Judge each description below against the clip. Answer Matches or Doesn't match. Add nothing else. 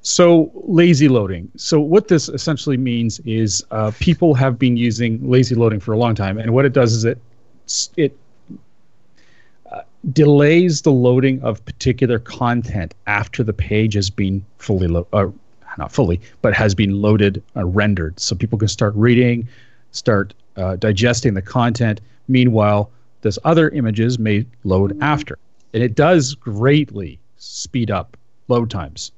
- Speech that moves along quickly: Doesn't match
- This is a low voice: Matches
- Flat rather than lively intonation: Doesn't match